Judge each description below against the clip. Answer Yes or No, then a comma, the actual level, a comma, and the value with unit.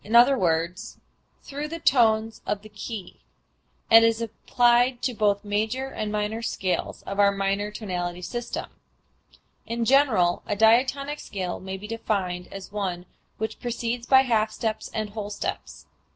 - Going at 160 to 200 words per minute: No, average, 145 wpm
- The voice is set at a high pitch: Yes, high, 220 Hz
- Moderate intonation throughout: Yes, average, 3.1 semitones